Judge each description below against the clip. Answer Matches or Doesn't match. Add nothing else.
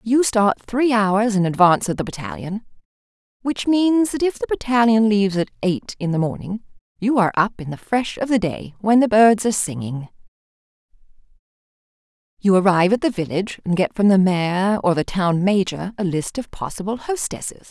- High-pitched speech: Matches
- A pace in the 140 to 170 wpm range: Doesn't match